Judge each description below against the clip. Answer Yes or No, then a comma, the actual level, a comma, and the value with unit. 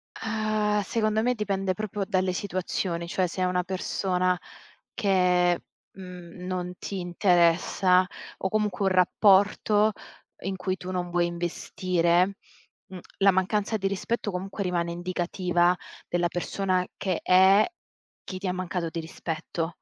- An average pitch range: No, narrow, 1.9 semitones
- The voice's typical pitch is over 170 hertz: Yes, medium, 185 Hz